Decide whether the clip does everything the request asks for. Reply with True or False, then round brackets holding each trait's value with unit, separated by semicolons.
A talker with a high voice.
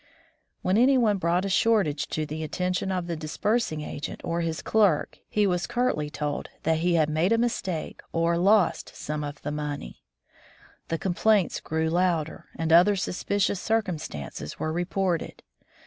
False (170 Hz)